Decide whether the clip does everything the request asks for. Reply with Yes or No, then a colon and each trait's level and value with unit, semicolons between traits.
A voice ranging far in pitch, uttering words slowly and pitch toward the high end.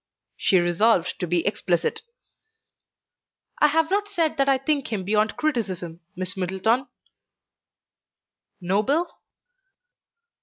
Yes: wide, 7.8 semitones; slow, 105 wpm; high, 215 Hz